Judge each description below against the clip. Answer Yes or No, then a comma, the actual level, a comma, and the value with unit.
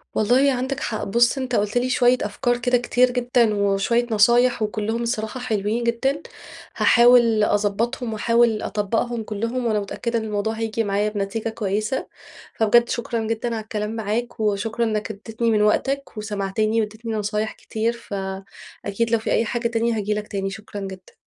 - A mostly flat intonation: Yes, narrow, 2.2 semitones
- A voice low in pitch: No, high, 225 Hz